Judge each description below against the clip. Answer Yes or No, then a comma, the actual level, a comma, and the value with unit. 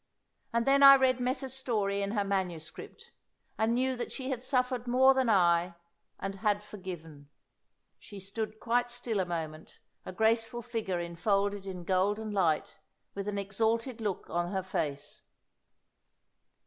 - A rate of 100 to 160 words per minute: Yes, average, 150 wpm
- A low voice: No, high, 205 Hz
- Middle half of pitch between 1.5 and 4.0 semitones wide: No, average, 4.5 semitones